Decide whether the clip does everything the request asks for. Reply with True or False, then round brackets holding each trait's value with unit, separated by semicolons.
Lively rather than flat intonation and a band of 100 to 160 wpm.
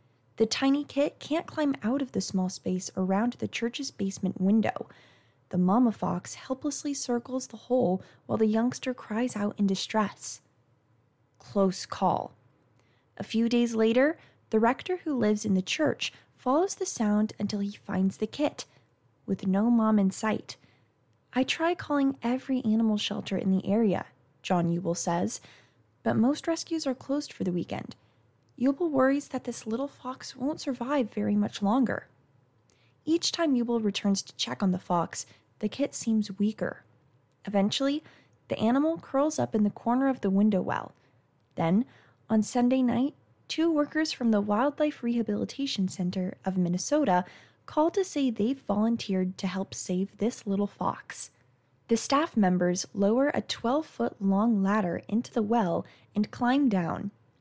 True (5.9 semitones; 155 wpm)